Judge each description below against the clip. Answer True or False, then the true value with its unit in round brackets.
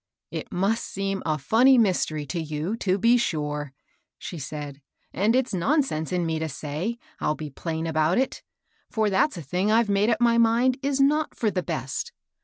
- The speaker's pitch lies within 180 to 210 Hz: True (190 Hz)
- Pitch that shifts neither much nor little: False (7.0 semitones)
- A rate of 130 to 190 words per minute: False (200 wpm)